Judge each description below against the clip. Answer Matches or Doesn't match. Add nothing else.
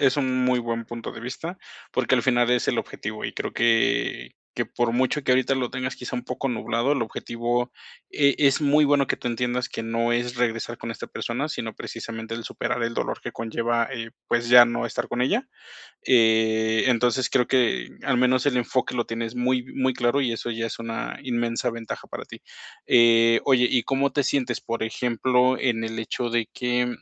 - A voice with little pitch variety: Matches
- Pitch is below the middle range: Matches